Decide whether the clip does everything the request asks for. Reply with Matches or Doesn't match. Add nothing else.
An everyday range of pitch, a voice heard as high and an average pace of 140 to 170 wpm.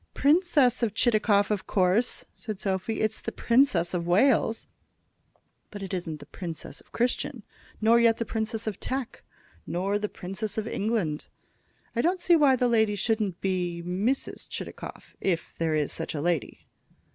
Matches